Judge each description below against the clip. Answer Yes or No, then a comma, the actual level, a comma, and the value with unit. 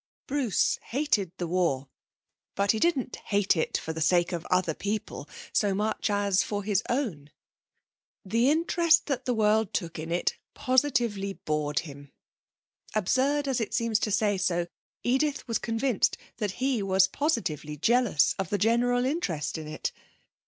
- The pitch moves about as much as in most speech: No, wide, 6.0 semitones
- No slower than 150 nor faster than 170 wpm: Yes, average, 155 wpm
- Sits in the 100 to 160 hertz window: No, high, 210 Hz